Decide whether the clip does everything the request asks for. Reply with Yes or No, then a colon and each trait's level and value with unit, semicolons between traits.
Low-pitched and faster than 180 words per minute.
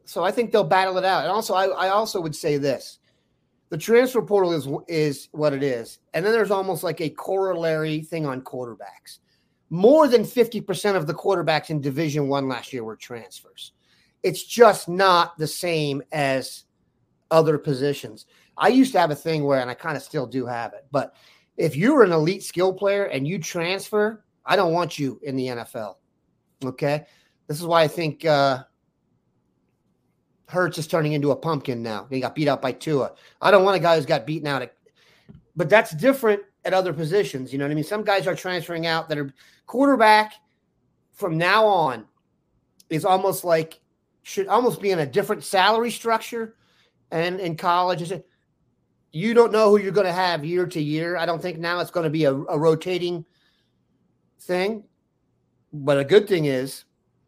No: medium, 170 Hz; average, 190 wpm